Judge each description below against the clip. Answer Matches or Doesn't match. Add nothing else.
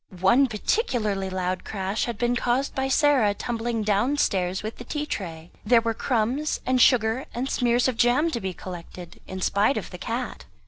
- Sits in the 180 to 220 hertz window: Doesn't match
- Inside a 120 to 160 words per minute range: Doesn't match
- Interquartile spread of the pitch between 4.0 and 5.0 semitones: Matches